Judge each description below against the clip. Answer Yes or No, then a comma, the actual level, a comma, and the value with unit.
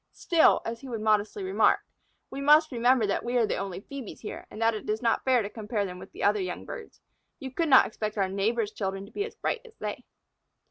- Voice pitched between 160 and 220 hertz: No, high, 230 Hz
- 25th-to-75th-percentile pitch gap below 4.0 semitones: No, average, 4.6 semitones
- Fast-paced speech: Yes, fast, 245 wpm